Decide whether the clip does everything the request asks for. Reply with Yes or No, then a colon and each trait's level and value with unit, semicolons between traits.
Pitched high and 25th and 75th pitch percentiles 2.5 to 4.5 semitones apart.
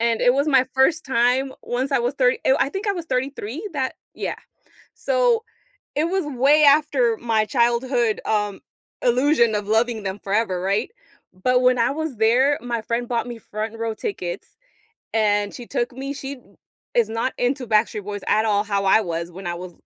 Yes: high, 240 Hz; average, 3.9 semitones